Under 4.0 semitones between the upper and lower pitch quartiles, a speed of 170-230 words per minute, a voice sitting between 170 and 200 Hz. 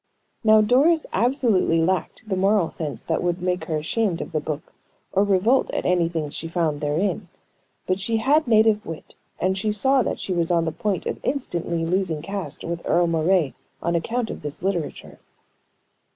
No: average, 4.5 semitones; average, 180 wpm; medium, 185 Hz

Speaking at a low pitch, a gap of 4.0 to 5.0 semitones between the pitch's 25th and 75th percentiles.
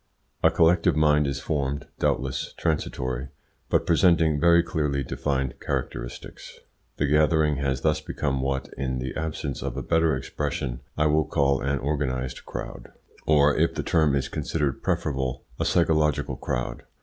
No: very low, 70 Hz; narrow, 2.6 semitones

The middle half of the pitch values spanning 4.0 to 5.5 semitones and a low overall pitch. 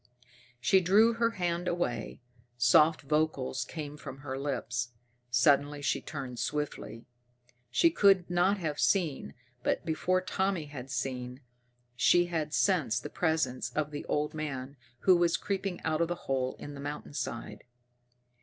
No: average, 5.0 semitones; medium, 150 Hz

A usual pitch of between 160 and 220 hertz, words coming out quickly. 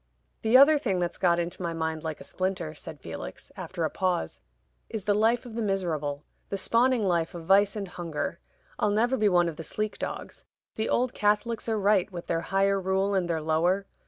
Yes: high, 190 Hz; fast, 210 wpm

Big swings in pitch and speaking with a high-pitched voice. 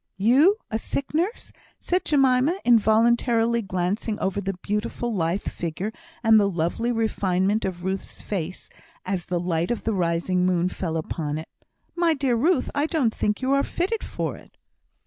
Yes: wide, 5.7 semitones; high, 215 Hz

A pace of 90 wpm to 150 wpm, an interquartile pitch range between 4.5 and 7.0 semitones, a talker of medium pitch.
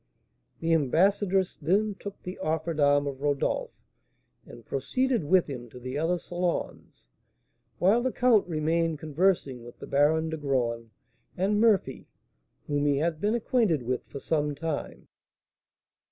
Yes: average, 140 wpm; average, 4.9 semitones; medium, 160 Hz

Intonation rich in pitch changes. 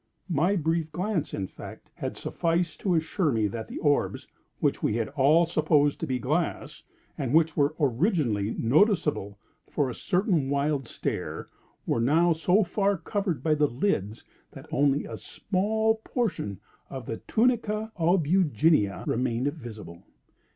Yes: wide, 5.8 semitones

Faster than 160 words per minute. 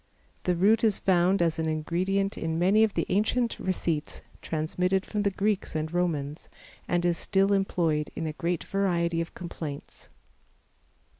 No: average, 155 wpm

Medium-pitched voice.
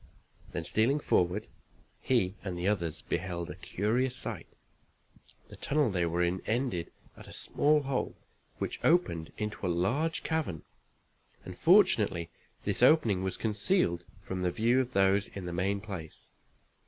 No: low, 100 Hz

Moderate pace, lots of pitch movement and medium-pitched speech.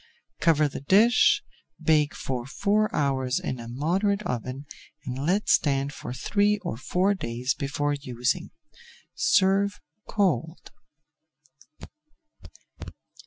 No: slow, 105 wpm; wide, 6.9 semitones; medium, 145 Hz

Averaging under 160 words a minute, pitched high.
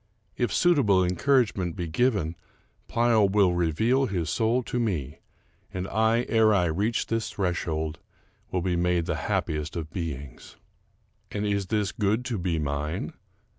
No: average, 145 wpm; very low, 95 Hz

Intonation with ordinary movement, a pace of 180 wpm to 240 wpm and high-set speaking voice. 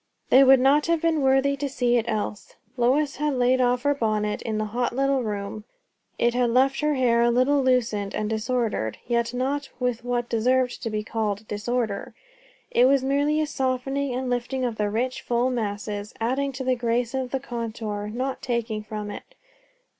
Yes: average, 3.1 semitones; average, 190 wpm; high, 245 Hz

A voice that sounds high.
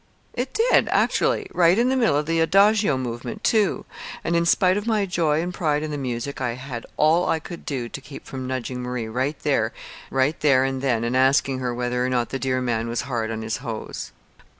No: low, 135 Hz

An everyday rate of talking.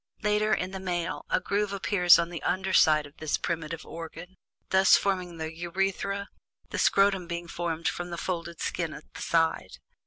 Yes: average, 180 wpm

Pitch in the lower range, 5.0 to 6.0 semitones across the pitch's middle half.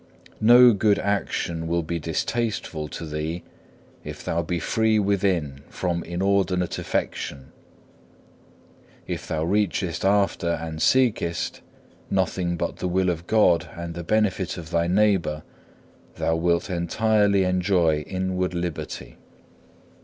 No: very low, 90 Hz; average, 3.1 semitones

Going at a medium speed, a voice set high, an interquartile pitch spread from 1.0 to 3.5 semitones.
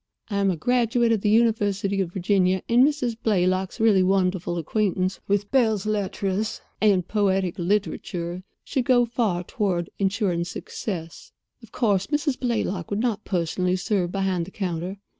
Yes: average, 150 wpm; high, 195 Hz; average, 3.2 semitones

